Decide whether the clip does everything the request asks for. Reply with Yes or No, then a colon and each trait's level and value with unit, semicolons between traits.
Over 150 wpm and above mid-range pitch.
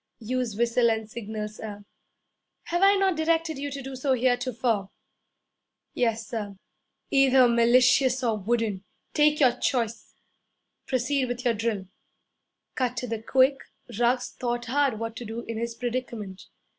No: average, 145 wpm; high, 240 Hz